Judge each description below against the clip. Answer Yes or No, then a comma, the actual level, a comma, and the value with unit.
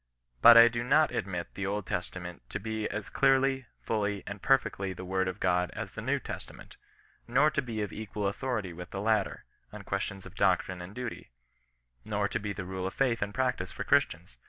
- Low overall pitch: Yes, low, 105 Hz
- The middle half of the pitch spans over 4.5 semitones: No, average, 3.9 semitones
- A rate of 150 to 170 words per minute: No, fast, 205 wpm